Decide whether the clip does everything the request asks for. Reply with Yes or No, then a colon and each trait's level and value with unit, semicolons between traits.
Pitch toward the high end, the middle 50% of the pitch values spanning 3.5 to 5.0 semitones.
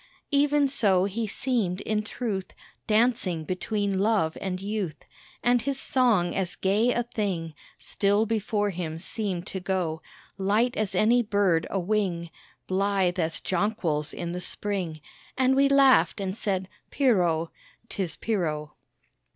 Yes: high, 200 Hz; average, 3.9 semitones